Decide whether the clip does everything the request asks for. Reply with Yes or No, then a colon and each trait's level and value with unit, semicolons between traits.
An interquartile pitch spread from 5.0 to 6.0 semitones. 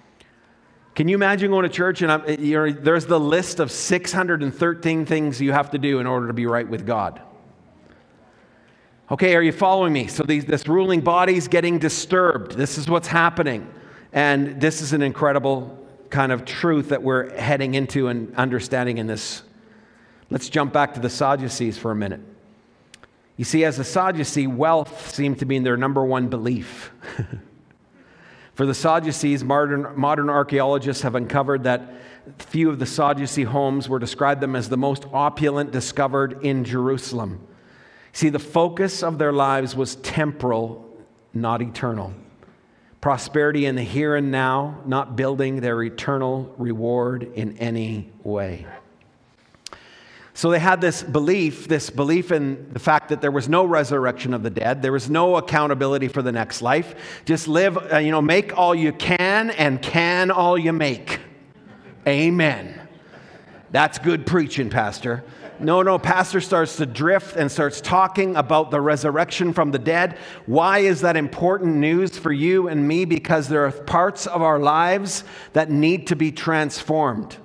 No: average, 4.2 semitones